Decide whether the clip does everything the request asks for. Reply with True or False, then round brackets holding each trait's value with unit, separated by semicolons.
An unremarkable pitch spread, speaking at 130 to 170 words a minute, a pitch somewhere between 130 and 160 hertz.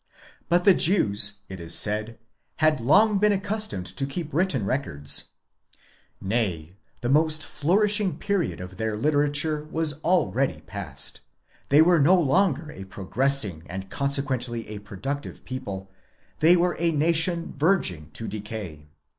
False (8.4 semitones; 135 wpm; 140 Hz)